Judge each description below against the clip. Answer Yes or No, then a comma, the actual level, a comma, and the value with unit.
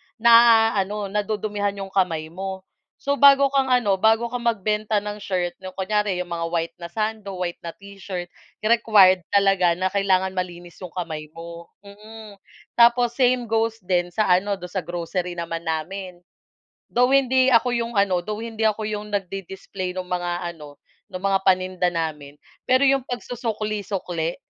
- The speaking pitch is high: Yes, high, 195 Hz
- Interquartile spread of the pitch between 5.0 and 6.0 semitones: No, average, 3.7 semitones